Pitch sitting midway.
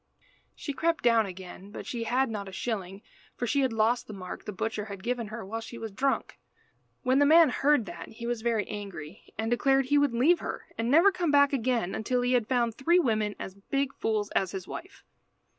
No: high, 235 Hz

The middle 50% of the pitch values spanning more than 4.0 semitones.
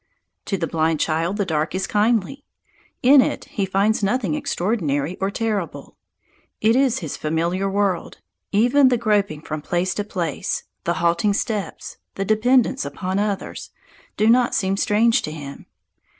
Yes: average, 4.4 semitones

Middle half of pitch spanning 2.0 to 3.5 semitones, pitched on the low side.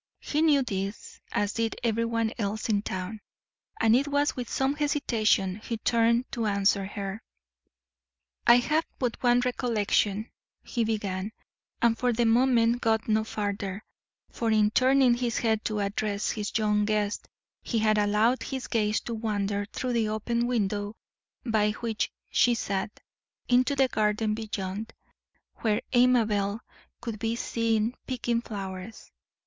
No: narrow, 2.5 semitones; high, 220 Hz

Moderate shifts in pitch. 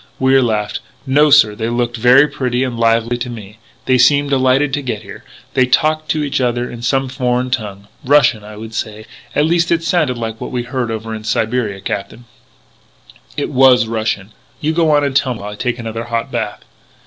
Yes: average, 3.3 semitones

